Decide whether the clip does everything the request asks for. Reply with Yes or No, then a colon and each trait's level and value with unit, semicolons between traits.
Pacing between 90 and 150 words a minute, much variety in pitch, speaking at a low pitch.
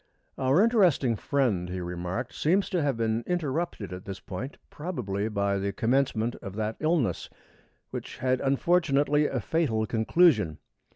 Yes: average, 140 wpm; wide, 7.0 semitones; low, 125 Hz